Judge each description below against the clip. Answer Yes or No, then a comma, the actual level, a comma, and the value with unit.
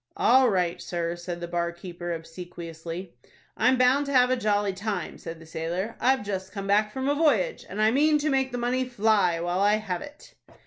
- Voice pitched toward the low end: No, high, 200 Hz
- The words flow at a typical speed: No, fast, 210 wpm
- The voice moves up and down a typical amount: No, wide, 6.4 semitones